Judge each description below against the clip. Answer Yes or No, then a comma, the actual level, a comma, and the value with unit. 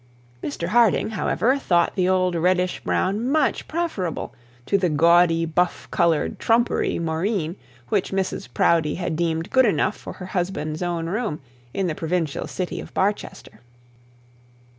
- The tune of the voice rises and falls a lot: No, average, 3.3 semitones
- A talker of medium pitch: Yes, medium, 180 Hz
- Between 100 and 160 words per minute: Yes, average, 140 wpm